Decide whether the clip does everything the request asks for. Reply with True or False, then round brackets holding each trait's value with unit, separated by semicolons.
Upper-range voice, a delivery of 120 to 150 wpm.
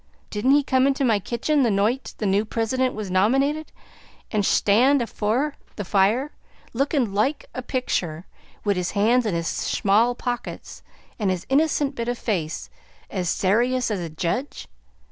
False (230 Hz; 165 wpm)